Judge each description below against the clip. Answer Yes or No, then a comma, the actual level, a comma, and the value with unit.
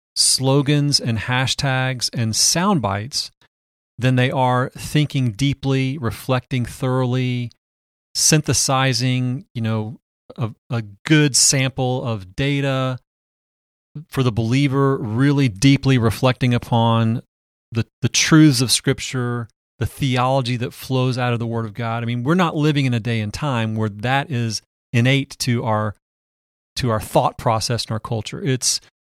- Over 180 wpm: No, average, 140 wpm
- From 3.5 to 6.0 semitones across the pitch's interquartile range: No, average, 3.0 semitones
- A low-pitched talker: Yes, low, 125 Hz